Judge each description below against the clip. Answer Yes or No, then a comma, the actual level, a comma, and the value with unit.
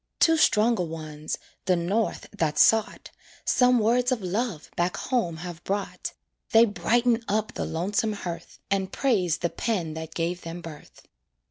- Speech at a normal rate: Yes, average, 150 wpm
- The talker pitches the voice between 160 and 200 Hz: Yes, high, 190 Hz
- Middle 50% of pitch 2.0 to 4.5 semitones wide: No, average, 5.2 semitones